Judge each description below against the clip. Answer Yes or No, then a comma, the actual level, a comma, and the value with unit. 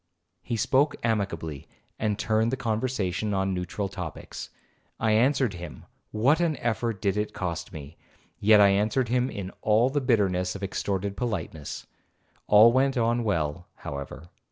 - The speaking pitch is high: No, low, 105 Hz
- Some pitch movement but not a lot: Yes, average, 4.4 semitones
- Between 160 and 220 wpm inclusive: No, average, 140 wpm